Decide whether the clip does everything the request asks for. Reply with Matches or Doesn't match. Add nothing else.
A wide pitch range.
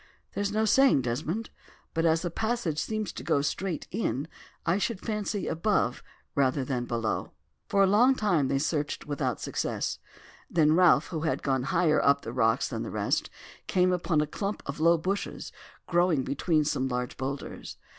Matches